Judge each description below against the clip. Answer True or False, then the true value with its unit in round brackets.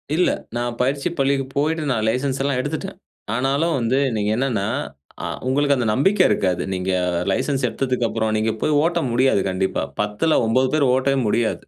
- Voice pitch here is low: True (130 Hz)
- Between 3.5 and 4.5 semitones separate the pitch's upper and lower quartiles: True (4.0 semitones)